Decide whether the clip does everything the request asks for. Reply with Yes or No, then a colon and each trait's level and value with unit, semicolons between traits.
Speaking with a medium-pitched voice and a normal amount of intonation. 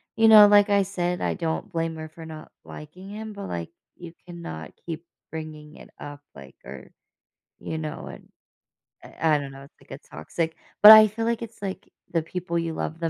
Yes: medium, 165 Hz; average, 4.4 semitones